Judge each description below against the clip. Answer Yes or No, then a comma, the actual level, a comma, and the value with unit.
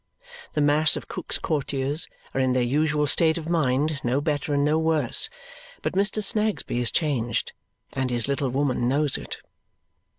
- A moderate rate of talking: Yes, average, 165 wpm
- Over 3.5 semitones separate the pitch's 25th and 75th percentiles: No, average, 3.2 semitones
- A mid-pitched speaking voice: Yes, medium, 145 Hz